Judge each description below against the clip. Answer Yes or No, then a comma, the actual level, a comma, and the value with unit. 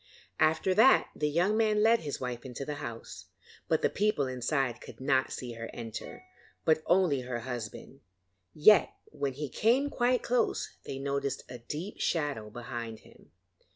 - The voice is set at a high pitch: No, medium, 140 Hz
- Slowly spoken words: No, average, 160 wpm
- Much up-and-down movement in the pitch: Yes, wide, 6.9 semitones